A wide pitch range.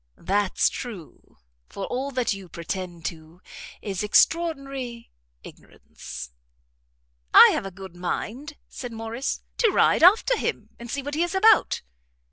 Yes: wide, 7.1 semitones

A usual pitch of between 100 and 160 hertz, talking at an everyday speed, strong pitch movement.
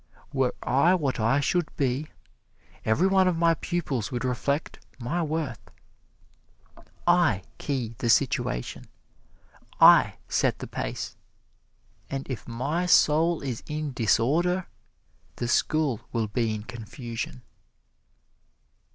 No: low, 135 Hz; slow, 115 wpm; wide, 5.7 semitones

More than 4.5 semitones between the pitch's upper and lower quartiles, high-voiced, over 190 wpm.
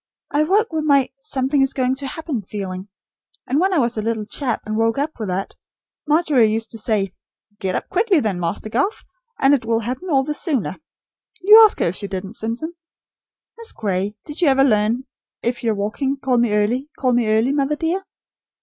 Yes: wide, 5.4 semitones; very high, 250 Hz; average, 200 wpm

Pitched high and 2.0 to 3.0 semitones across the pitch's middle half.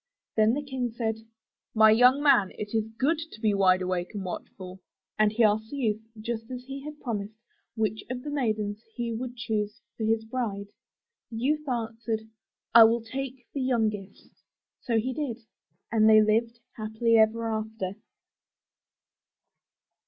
Yes: high, 225 Hz; narrow, 2.4 semitones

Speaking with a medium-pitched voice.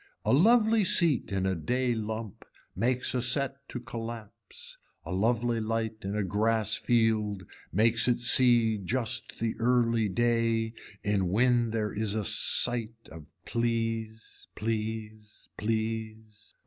No: low, 115 Hz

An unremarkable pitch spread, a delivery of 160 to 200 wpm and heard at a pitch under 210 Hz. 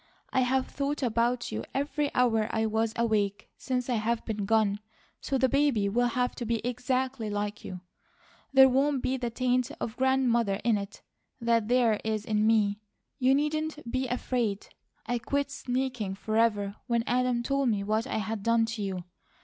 No: average, 3.0 semitones; average, 175 wpm; high, 235 Hz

